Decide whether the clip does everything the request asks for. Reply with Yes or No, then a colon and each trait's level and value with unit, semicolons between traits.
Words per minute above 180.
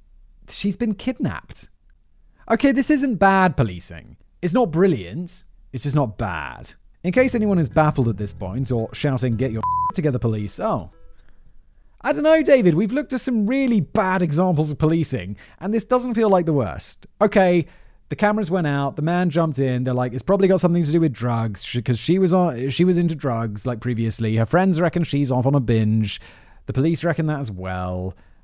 Yes: average, 195 wpm